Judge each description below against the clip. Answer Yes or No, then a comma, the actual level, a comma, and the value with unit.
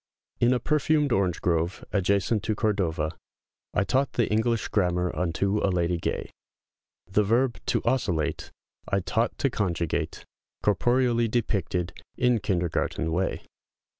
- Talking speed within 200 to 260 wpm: No, slow, 135 wpm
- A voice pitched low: Yes, low, 100 Hz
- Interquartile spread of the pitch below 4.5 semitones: No, average, 5.0 semitones